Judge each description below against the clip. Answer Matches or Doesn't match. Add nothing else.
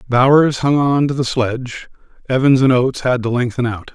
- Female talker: Doesn't match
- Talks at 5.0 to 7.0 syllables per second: Matches